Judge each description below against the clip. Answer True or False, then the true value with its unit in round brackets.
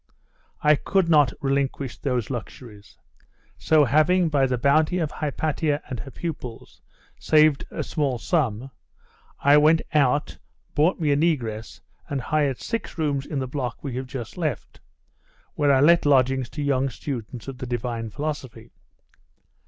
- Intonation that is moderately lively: True (3.3 semitones)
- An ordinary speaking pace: True (150 wpm)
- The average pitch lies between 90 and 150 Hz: True (140 Hz)